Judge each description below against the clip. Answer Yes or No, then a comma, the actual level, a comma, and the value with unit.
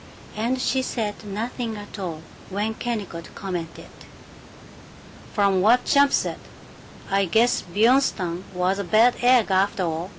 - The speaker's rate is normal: No, slow, 130 wpm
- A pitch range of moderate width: Yes, average, 4.1 semitones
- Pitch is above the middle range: Yes, high, 205 Hz